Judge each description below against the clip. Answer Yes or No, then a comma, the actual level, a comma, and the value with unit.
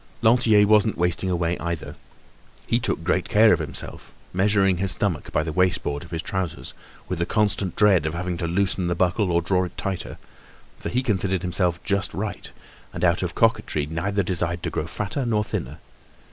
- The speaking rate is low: No, average, 190 wpm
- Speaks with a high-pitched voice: No, very low, 90 Hz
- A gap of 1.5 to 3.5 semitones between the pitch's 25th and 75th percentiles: Yes, average, 2.9 semitones